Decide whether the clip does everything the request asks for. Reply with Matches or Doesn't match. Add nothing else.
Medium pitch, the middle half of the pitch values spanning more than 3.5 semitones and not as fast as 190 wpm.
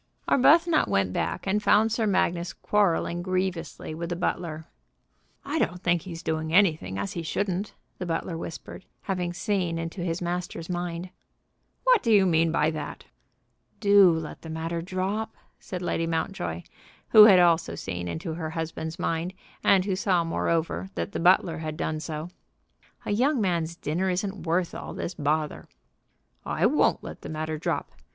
Doesn't match